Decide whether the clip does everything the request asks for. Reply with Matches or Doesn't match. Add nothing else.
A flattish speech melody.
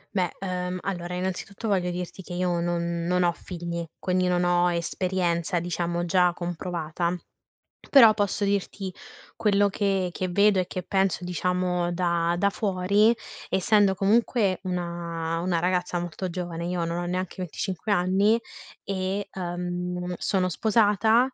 Matches